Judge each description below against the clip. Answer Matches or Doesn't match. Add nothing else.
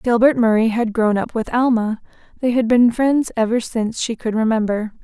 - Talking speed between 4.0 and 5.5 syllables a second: Matches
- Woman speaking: Matches